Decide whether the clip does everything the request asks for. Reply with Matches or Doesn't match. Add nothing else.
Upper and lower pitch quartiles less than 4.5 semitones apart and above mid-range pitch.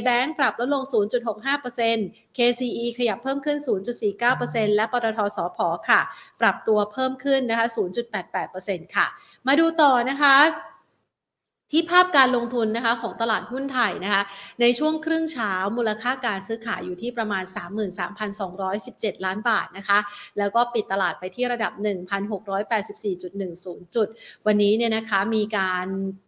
Matches